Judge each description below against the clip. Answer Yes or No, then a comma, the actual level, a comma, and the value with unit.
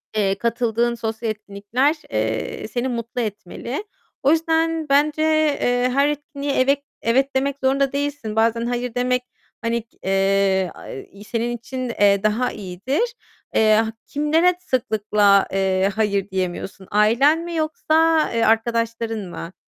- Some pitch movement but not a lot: Yes, average, 4.9 semitones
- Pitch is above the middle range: Yes, high, 235 Hz